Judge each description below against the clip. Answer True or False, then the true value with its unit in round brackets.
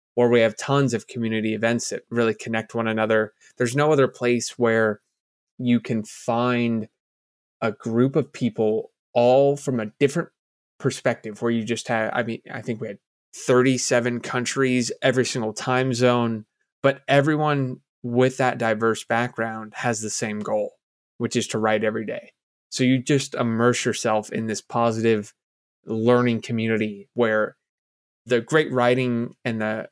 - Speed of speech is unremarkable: True (155 wpm)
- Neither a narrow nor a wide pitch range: False (2.2 semitones)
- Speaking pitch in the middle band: False (120 Hz)